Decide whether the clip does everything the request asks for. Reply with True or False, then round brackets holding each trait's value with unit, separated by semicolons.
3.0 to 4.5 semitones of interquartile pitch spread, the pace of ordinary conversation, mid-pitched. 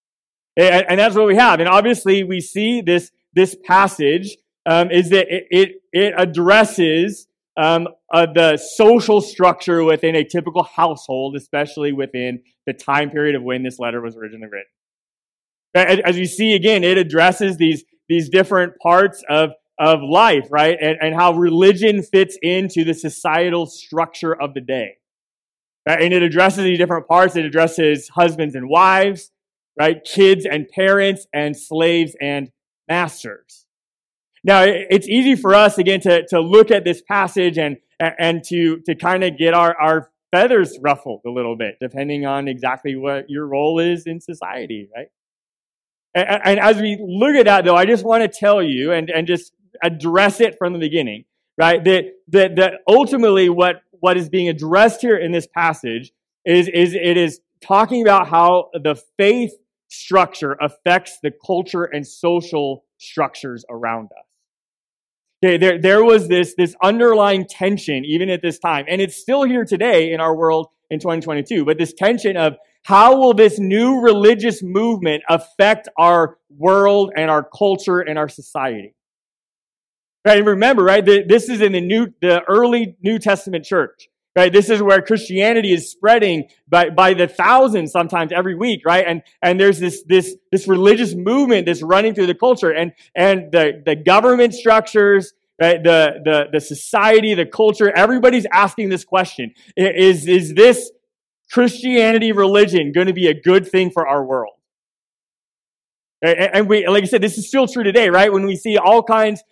True (3.7 semitones; 165 wpm; 180 Hz)